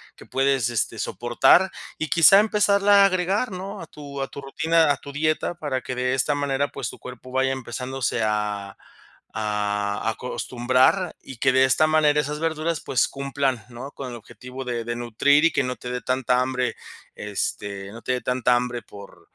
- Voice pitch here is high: No, low, 130 Hz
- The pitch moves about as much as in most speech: Yes, average, 3.6 semitones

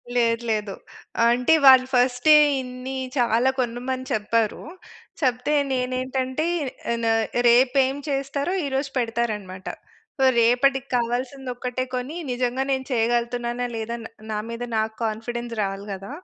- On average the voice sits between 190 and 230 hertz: No, high, 245 Hz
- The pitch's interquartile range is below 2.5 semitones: Yes, narrow, 2.0 semitones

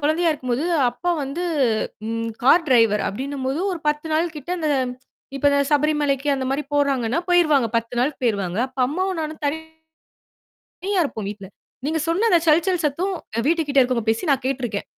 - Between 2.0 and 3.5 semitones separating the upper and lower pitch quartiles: No, average, 4.3 semitones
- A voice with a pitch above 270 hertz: Yes, very high, 285 Hz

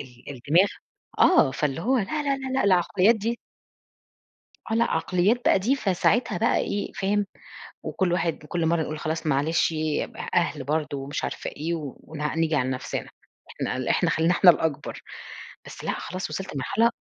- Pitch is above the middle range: No, medium, 170 Hz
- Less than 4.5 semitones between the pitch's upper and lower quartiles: No, average, 5.1 semitones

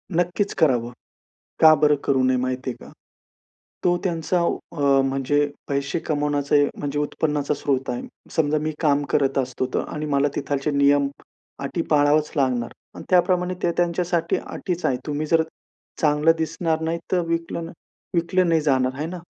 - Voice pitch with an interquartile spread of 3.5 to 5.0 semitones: No, average, 3.0 semitones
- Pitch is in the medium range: Yes, medium, 150 Hz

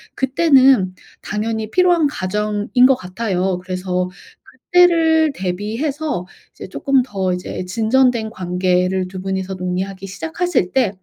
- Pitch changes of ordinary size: No, wide, 6.4 semitones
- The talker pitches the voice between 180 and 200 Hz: No, high, 210 Hz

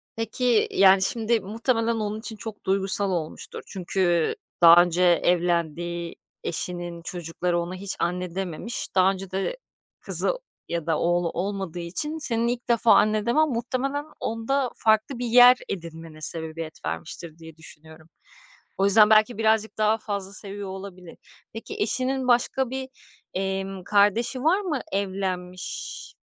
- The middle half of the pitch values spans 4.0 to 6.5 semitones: Yes, average, 4.7 semitones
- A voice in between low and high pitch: No, high, 195 Hz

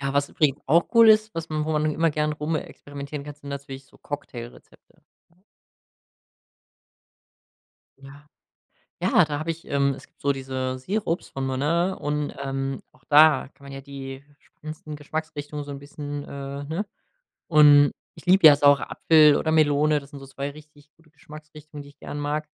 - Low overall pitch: No, medium, 145 Hz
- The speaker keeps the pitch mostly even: Yes, narrow, 1.7 semitones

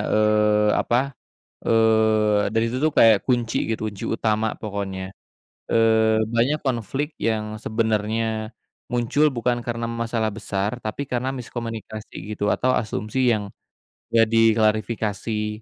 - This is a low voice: Yes, low, 110 Hz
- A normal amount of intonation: No, narrow, 1.7 semitones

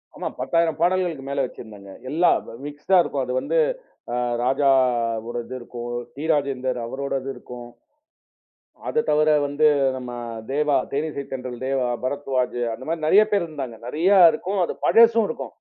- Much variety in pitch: No, average, 3.9 semitones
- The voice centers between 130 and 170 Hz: Yes, medium, 140 Hz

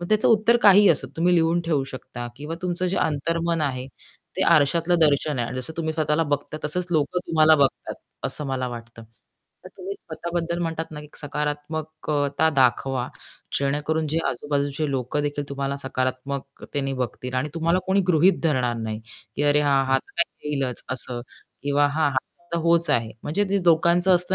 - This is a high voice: No, medium, 150 Hz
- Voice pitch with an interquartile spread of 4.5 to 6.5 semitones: No, average, 3.5 semitones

